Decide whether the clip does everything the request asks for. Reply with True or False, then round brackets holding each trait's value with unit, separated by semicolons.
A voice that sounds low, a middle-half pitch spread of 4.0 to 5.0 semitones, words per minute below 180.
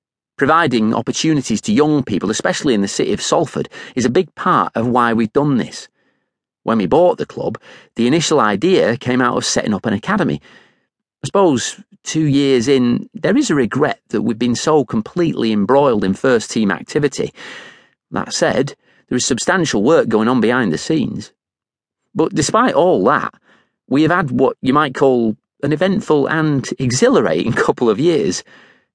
True (130 Hz; 4.6 semitones; 170 wpm)